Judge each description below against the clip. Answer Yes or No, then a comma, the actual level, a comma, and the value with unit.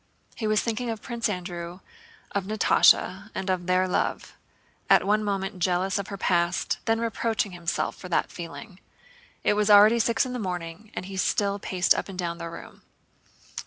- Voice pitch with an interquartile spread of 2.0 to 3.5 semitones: Yes, average, 3.1 semitones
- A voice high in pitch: Yes, high, 195 Hz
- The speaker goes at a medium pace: Yes, average, 180 wpm